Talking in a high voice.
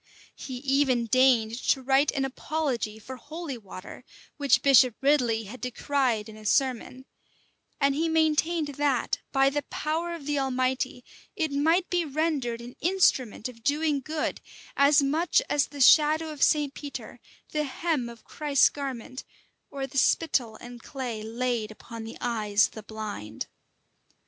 Yes: very high, 270 Hz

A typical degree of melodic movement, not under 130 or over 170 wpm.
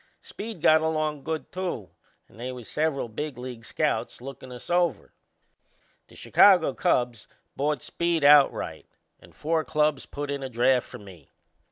Yes: average, 4.2 semitones; average, 155 wpm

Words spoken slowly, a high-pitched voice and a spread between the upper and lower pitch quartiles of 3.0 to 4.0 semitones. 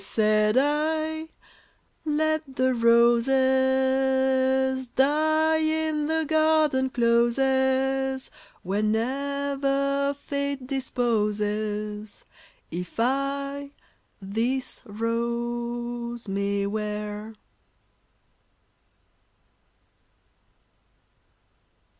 Yes: slow, 55 wpm; very high, 265 Hz; average, 3.4 semitones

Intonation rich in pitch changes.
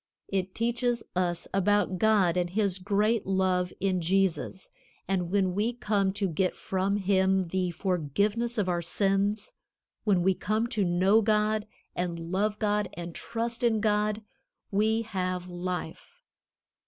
No: average, 2.7 semitones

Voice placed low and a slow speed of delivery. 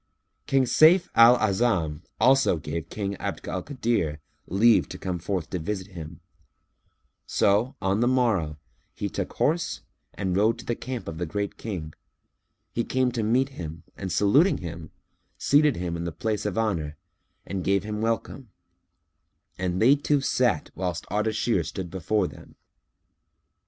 No: low, 100 Hz; average, 155 wpm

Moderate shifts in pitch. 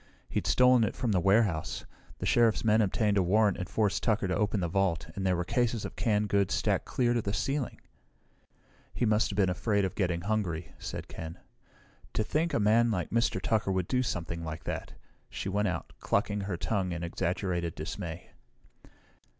Yes: average, 3.8 semitones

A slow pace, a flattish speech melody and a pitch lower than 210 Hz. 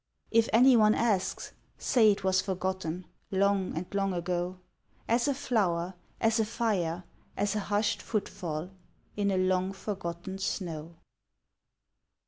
No: slow, 125 wpm; average, 3.0 semitones; high, 190 Hz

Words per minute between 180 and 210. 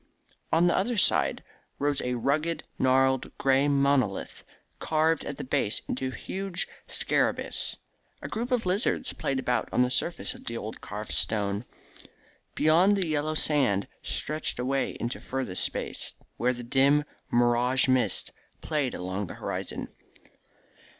No: average, 145 wpm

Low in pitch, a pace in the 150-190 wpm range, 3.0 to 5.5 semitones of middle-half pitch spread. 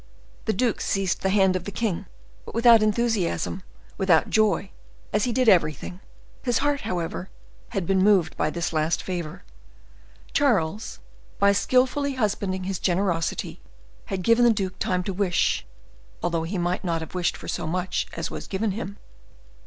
No: high, 190 Hz; average, 160 wpm; average, 3.6 semitones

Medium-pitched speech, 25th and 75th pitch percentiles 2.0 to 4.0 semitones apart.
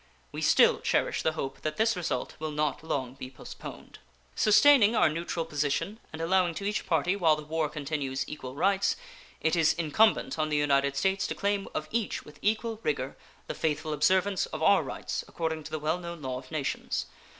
No: medium, 160 Hz; average, 4.4 semitones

